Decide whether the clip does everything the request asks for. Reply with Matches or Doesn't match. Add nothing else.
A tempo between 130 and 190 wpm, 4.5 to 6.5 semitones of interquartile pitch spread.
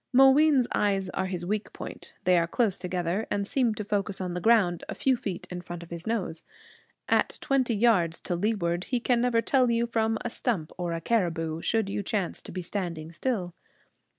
Doesn't match